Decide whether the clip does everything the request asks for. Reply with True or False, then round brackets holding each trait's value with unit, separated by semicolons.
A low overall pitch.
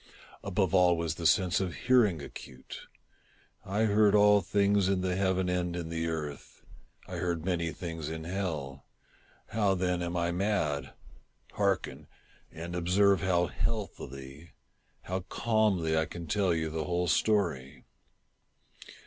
True (90 Hz)